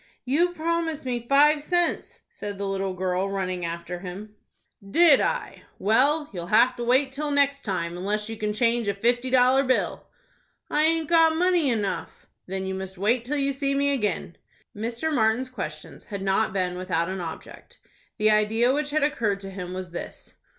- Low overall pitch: No, high, 225 Hz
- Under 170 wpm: No, average, 180 wpm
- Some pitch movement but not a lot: No, wide, 6.6 semitones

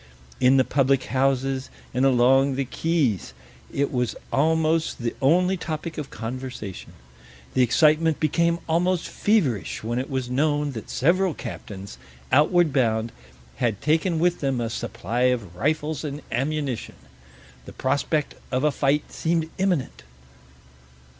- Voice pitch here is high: No, medium, 140 Hz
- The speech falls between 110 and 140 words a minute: Yes, slow, 135 wpm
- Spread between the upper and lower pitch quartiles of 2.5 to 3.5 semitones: No, average, 4.0 semitones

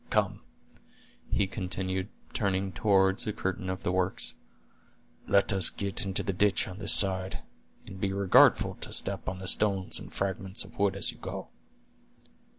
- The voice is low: Yes, very low, 95 Hz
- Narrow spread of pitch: Yes, narrow, 1.0 semitones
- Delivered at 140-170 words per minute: Yes, average, 160 wpm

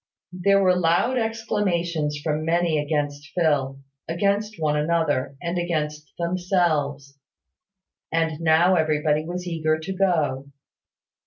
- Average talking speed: No, slow, 110 wpm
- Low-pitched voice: No, medium, 165 Hz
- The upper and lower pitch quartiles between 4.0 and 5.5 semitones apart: No, average, 3.1 semitones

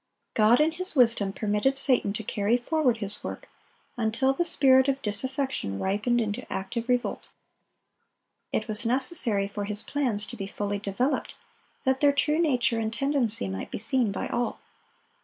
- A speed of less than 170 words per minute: Yes, average, 160 wpm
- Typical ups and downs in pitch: Yes, average, 4.4 semitones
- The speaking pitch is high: Yes, high, 235 Hz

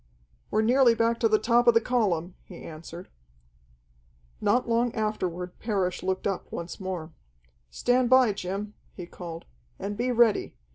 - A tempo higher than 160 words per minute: No, average, 150 wpm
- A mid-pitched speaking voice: No, high, 210 Hz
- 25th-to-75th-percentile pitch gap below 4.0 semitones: No, average, 4.6 semitones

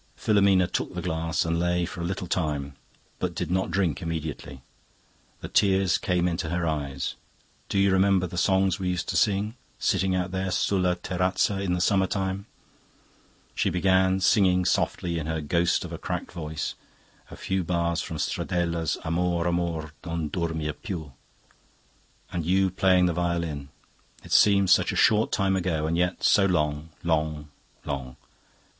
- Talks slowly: No, average, 165 wpm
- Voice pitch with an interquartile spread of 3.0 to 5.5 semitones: No, narrow, 2.6 semitones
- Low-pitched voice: Yes, very low, 90 Hz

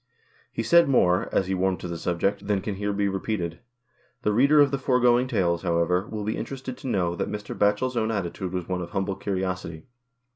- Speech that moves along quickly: Yes, fast, 210 wpm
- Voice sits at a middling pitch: No, low, 100 Hz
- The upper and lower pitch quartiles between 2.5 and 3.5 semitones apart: No, average, 4.1 semitones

